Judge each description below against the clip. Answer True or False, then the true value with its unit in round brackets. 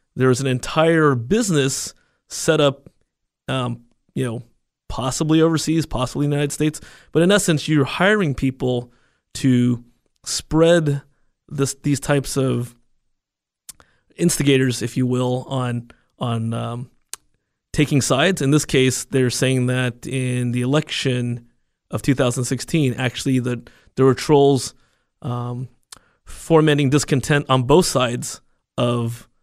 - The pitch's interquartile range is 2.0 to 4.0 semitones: True (3.1 semitones)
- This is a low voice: True (130 Hz)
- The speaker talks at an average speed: False (120 wpm)